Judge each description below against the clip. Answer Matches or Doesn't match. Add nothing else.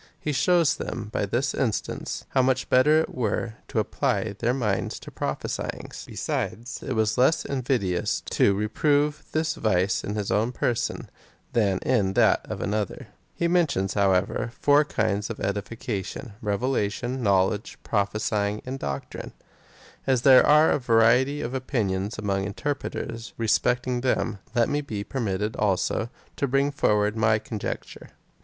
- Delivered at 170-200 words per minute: Doesn't match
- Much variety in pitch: Doesn't match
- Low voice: Matches